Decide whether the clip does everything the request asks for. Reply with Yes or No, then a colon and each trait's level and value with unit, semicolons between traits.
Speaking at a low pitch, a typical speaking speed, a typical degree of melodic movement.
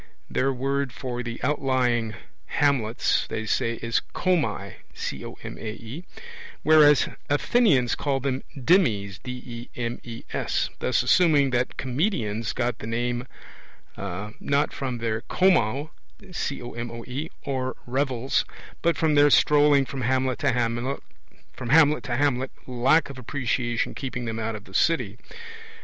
No: low, 130 Hz; slow, 105 wpm; average, 3.4 semitones